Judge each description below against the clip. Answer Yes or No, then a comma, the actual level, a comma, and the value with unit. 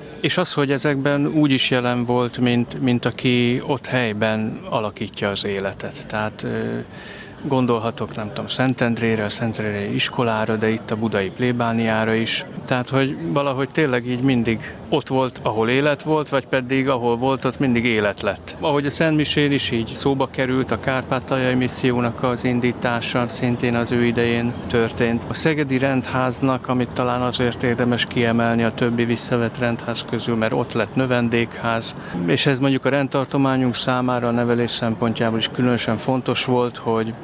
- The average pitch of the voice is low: Yes, low, 125 Hz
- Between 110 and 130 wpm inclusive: No, fast, 155 wpm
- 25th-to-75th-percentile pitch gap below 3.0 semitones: Yes, narrow, 2.5 semitones